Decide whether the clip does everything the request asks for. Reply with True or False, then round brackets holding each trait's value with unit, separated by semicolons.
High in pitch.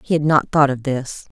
False (145 Hz)